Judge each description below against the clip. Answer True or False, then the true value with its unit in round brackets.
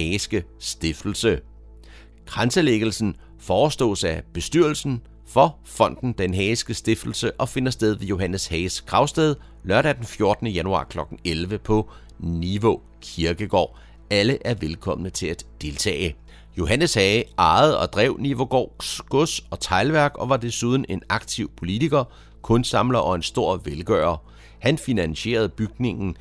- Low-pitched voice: True (105 Hz)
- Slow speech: True (130 wpm)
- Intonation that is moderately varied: False (6.1 semitones)